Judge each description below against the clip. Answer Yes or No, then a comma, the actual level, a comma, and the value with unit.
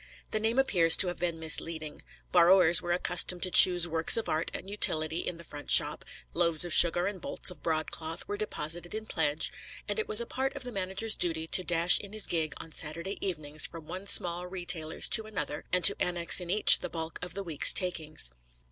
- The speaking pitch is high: No, medium, 175 Hz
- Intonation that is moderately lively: Yes, average, 3.0 semitones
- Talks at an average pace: No, fast, 210 wpm